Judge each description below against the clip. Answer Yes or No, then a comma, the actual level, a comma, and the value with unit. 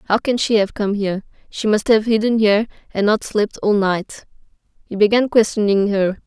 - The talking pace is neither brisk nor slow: Yes, average, 190 wpm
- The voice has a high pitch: Yes, high, 210 Hz